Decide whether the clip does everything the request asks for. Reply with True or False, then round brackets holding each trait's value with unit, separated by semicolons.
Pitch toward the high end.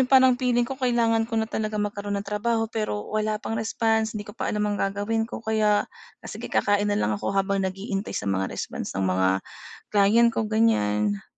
True (215 Hz)